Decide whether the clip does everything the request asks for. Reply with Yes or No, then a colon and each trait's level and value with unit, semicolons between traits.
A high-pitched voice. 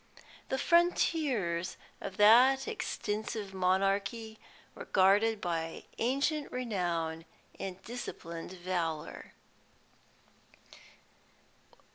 Yes: high, 200 Hz